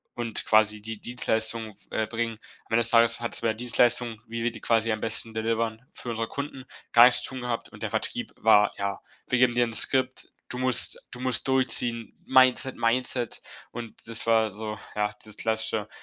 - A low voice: Yes, low, 115 Hz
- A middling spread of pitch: No, narrow, 1.7 semitones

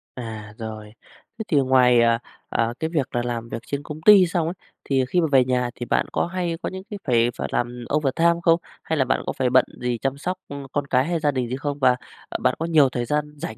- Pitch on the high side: No, low, 135 Hz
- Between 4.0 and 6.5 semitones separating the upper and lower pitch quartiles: Yes, average, 4.7 semitones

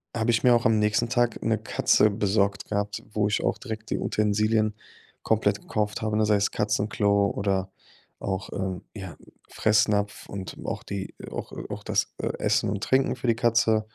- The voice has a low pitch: Yes, low, 105 Hz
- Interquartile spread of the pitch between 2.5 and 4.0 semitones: No, narrow, 1.5 semitones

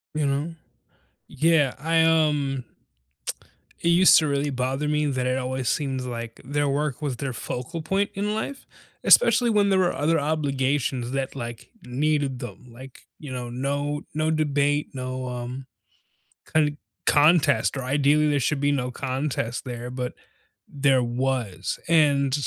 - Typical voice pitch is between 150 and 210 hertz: No, medium, 140 Hz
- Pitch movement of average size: Yes, average, 3.0 semitones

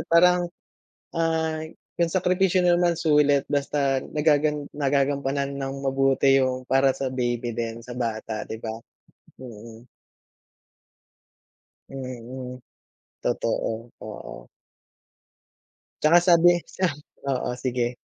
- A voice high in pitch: No, low, 135 Hz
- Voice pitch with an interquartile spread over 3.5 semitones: Yes, average, 4.2 semitones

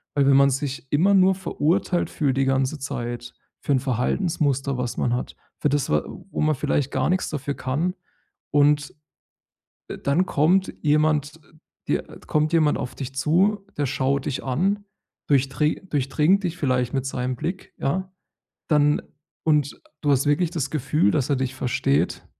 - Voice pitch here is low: No, medium, 145 Hz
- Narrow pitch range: No, average, 3.0 semitones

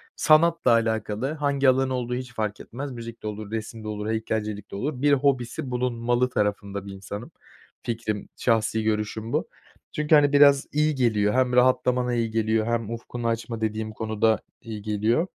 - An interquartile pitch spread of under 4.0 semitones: Yes, average, 2.9 semitones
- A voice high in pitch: No, low, 115 Hz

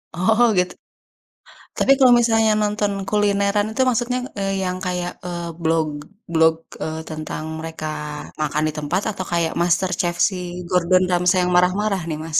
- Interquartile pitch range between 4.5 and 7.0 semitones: No, average, 4.0 semitones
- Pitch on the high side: No, medium, 180 Hz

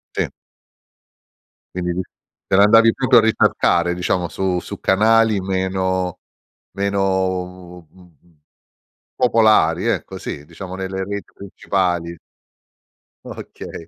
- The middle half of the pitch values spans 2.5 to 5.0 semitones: No, narrow, 2.1 semitones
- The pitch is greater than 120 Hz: No, very low, 95 Hz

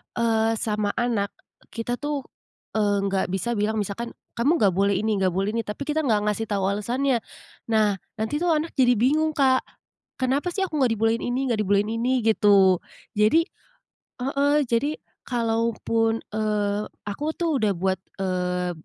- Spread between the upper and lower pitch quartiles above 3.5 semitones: Yes, average, 4.2 semitones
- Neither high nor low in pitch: No, high, 225 Hz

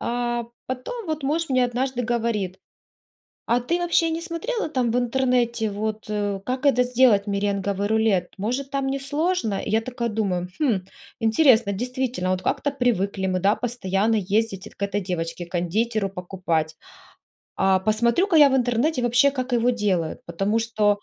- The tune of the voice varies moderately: Yes, average, 4.4 semitones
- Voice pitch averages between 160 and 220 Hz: No, high, 230 Hz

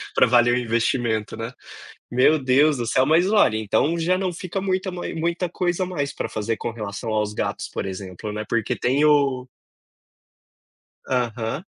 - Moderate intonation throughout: No, wide, 7.0 semitones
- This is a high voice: No, low, 125 Hz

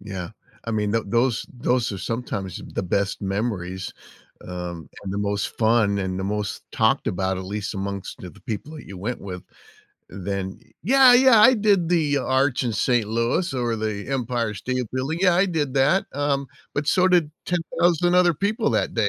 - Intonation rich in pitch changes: Yes, wide, 7.1 semitones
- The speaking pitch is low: Yes, low, 115 Hz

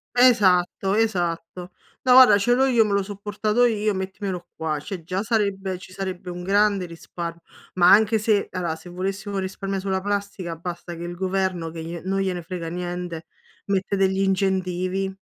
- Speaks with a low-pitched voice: No, high, 190 Hz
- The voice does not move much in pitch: Yes, narrow, 2.3 semitones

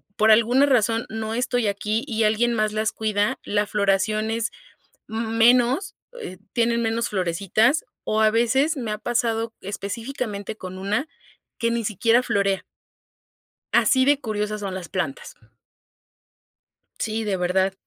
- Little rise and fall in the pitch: Yes, narrow, 2.3 semitones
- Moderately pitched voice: No, high, 220 Hz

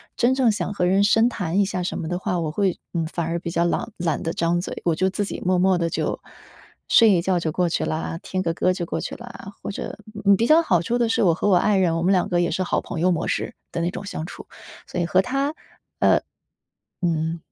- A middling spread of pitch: Yes, average, 3.0 semitones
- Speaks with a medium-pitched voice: Yes, medium, 180 Hz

